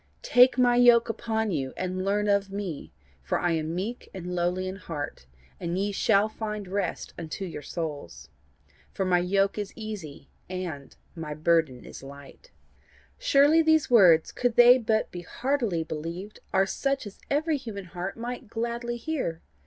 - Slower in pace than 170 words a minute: Yes, average, 160 wpm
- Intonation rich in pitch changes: Yes, wide, 5.7 semitones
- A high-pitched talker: Yes, high, 195 Hz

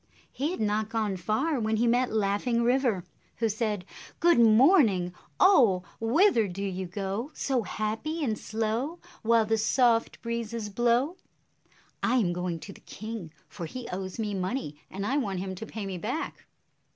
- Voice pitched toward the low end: No, high, 220 Hz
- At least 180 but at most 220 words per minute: No, average, 165 wpm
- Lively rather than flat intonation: No, average, 3.7 semitones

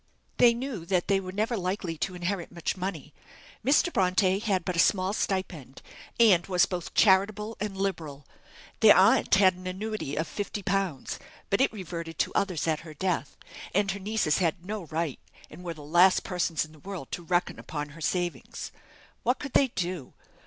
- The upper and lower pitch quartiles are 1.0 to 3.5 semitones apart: Yes, average, 3.0 semitones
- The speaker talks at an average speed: Yes, average, 180 wpm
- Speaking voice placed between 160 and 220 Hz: Yes, medium, 185 Hz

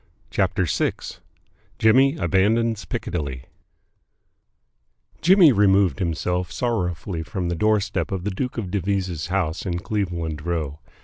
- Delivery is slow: Yes, slow, 115 wpm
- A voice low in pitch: Yes, very low, 95 Hz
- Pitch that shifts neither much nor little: Yes, average, 3.9 semitones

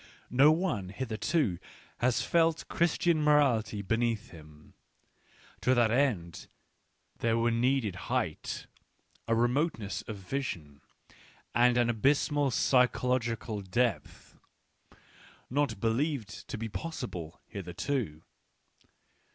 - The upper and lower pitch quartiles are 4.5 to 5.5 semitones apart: Yes, average, 4.9 semitones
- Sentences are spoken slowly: Yes, slow, 100 wpm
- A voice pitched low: Yes, low, 120 Hz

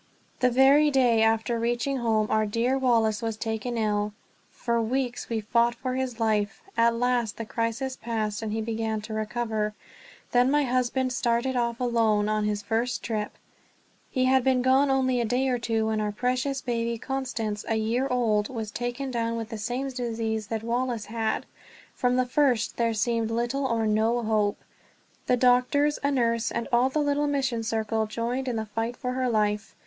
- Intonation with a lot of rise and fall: No, narrow, 2.4 semitones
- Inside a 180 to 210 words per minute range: Yes, average, 185 wpm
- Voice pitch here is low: No, high, 235 Hz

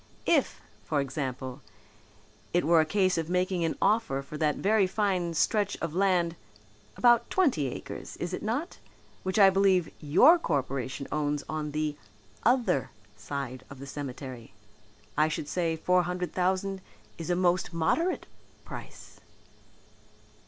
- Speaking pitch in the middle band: Yes, medium, 170 Hz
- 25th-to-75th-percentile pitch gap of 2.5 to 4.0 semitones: No, average, 4.7 semitones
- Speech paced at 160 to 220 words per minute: No, average, 140 wpm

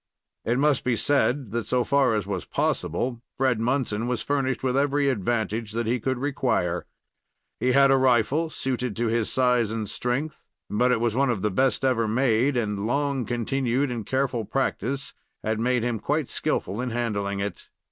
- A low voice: Yes, low, 120 Hz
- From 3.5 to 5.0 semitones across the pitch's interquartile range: No, average, 3.1 semitones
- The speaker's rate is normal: Yes, average, 185 wpm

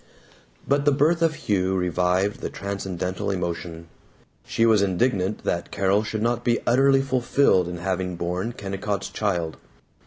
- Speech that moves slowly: No, average, 145 wpm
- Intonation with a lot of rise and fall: No, average, 4.7 semitones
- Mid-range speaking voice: No, low, 100 Hz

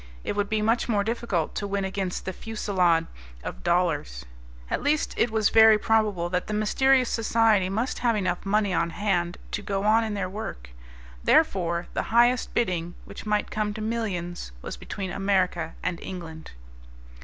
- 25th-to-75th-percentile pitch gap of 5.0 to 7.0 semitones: No, average, 3.8 semitones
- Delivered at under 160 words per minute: No, average, 170 wpm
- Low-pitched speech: No, high, 200 Hz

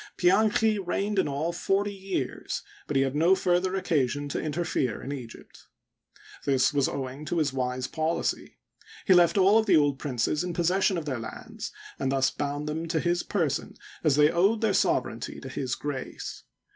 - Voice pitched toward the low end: No, medium, 155 Hz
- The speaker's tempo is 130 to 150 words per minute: No, average, 180 wpm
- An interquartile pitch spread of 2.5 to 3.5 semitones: No, average, 5.3 semitones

